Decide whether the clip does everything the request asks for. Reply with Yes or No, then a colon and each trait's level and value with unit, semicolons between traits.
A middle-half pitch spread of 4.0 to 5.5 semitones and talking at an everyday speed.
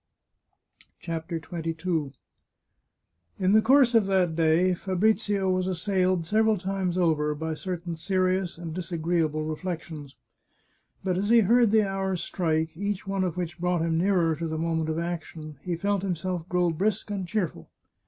No: average, 2.9 semitones; average, 155 wpm